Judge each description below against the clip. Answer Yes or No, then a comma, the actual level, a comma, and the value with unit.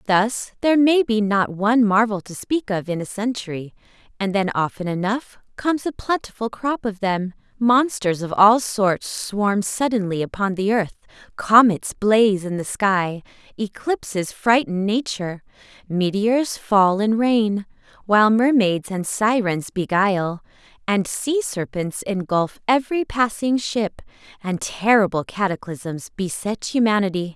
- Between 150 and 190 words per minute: No, slow, 135 wpm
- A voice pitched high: Yes, high, 210 Hz